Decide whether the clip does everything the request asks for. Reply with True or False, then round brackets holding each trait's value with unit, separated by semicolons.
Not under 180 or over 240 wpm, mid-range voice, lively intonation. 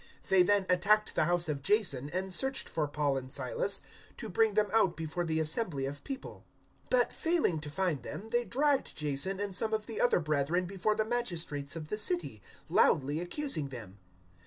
True (190 wpm; 180 Hz; 6.4 semitones)